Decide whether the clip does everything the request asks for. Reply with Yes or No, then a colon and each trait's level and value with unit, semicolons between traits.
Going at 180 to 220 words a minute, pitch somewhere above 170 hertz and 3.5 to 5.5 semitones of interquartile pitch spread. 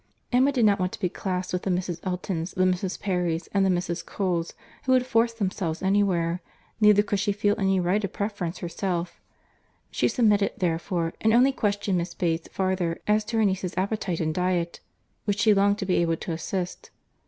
No: average, 190 wpm; high, 190 Hz; average, 2.7 semitones